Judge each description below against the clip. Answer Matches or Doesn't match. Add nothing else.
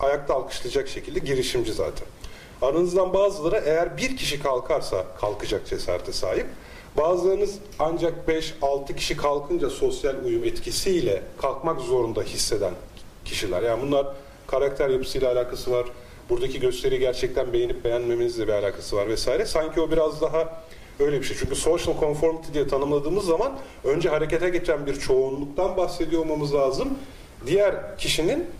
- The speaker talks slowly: Doesn't match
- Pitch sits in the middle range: Matches